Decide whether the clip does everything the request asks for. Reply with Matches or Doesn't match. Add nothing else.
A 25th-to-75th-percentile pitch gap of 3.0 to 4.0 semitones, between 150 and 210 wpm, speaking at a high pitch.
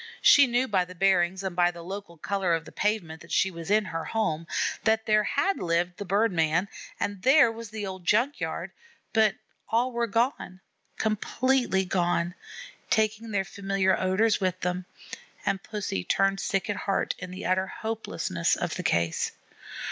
Matches